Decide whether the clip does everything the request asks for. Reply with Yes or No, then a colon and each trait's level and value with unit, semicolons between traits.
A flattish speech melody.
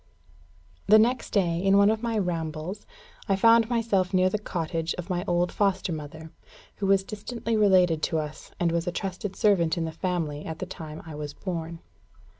No: average, 3.8 semitones